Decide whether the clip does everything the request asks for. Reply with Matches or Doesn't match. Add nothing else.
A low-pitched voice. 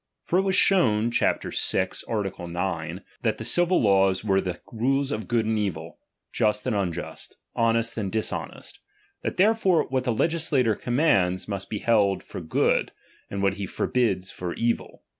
Matches